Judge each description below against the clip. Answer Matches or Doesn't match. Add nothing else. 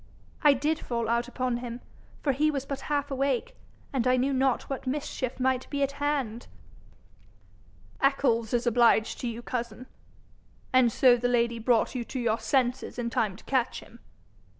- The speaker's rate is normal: Matches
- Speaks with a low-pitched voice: Doesn't match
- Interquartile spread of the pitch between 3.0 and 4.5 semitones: Doesn't match